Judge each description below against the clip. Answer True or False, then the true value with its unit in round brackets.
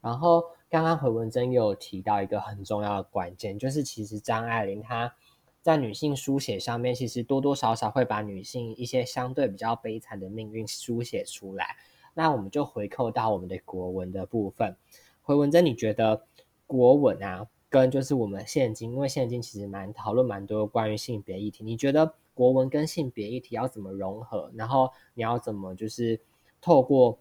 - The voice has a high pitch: False (115 Hz)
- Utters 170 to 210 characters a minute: False (290 characters per minute)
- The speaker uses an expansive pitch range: False (3.6 semitones)